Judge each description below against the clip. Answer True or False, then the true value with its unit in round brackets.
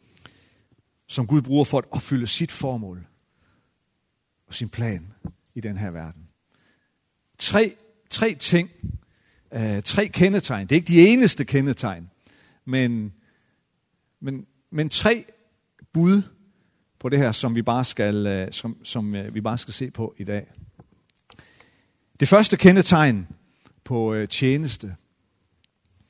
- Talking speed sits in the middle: False (120 wpm)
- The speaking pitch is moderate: False (120 Hz)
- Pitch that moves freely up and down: True (6.7 semitones)